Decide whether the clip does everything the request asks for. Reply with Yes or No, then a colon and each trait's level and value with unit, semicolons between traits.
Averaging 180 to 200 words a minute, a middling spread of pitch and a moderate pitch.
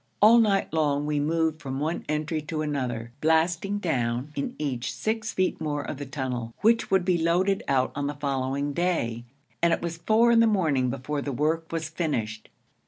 Yes: average, 190 wpm; average, 4.1 semitones; medium, 155 Hz